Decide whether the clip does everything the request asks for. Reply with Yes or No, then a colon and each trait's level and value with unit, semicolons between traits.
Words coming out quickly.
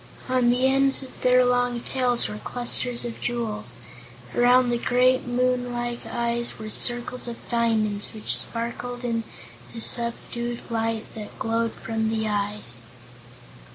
No: average, 140 wpm